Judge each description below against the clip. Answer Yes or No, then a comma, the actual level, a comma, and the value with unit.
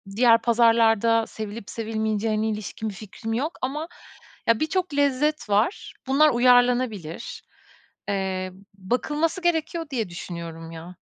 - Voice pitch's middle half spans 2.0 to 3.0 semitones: No, average, 4.9 semitones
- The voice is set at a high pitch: Yes, high, 230 Hz